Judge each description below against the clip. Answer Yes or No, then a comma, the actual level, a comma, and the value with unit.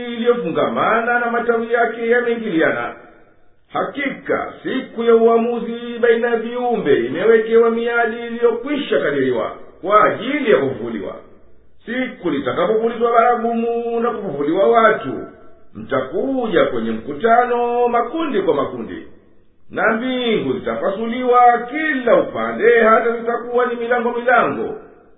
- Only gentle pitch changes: Yes, narrow, 1.1 semitones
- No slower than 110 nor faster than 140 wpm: No, slow, 100 wpm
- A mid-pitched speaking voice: No, high, 235 Hz